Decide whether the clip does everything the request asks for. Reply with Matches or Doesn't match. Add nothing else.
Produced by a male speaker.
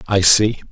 Matches